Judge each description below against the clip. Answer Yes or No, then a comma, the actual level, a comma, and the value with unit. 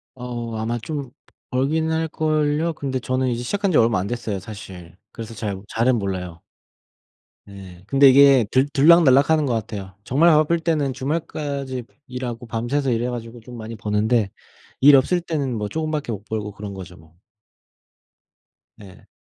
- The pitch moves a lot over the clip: No, average, 5.0 semitones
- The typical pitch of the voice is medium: No, low, 125 Hz